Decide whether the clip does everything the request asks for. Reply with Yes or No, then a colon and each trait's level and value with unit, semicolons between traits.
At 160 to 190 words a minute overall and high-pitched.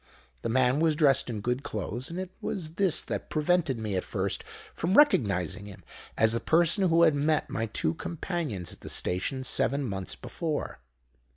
No: average, 180 wpm; medium, 140 Hz